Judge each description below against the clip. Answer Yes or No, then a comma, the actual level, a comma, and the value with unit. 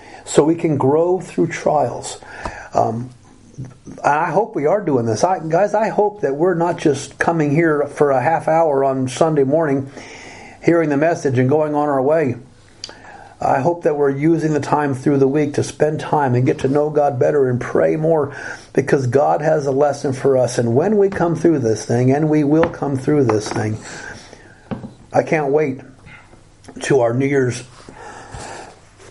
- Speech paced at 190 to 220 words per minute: No, average, 180 wpm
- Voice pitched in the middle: Yes, medium, 145 Hz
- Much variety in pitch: No, average, 3.9 semitones